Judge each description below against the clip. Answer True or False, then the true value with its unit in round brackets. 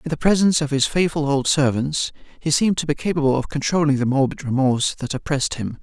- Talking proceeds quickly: True (215 wpm)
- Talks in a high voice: False (145 Hz)